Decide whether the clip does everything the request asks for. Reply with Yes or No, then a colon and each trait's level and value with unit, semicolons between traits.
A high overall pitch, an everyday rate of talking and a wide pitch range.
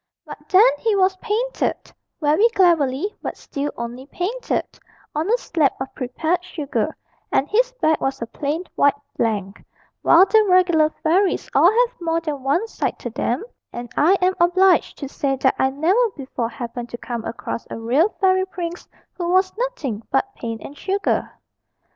Yes: very high, 325 Hz; average, 170 wpm; wide, 6.2 semitones